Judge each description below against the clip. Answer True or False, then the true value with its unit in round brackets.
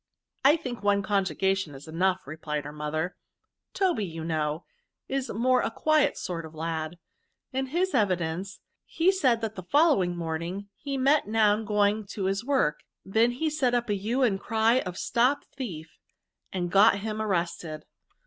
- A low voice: False (200 Hz)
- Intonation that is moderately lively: False (6.5 semitones)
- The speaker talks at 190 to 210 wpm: False (175 wpm)